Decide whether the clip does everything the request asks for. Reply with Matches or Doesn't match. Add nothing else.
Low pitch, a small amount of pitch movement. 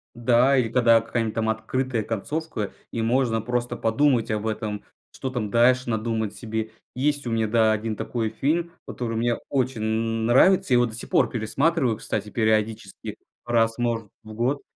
Matches